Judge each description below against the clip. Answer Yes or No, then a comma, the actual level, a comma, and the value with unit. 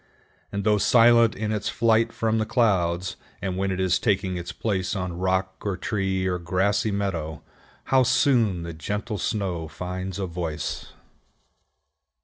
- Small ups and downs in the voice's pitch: No, average, 3.1 semitones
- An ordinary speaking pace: Yes, average, 150 wpm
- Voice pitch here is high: No, very low, 95 Hz